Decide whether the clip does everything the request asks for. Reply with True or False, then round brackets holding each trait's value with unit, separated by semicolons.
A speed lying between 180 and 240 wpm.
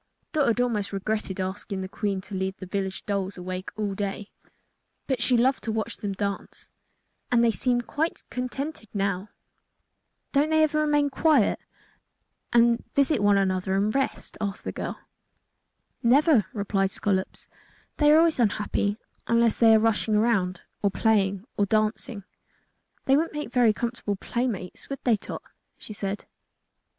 False (155 wpm)